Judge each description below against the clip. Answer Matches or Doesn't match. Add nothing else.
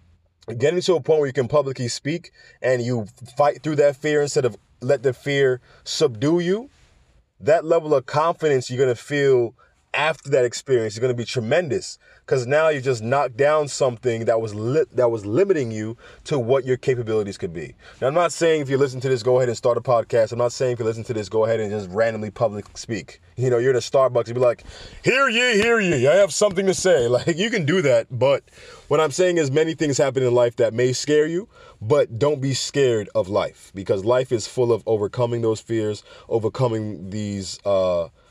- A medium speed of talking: Doesn't match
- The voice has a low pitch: Matches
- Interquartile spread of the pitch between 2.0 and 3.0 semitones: Doesn't match